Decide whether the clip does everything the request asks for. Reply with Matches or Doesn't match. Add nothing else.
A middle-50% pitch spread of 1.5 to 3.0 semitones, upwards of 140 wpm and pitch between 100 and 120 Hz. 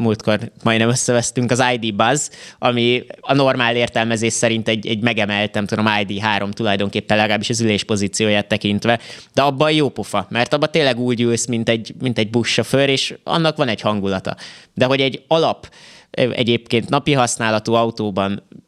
Matches